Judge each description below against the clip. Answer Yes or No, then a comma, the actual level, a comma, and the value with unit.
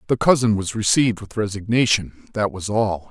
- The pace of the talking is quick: No, average, 175 wpm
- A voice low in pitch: Yes, low, 105 Hz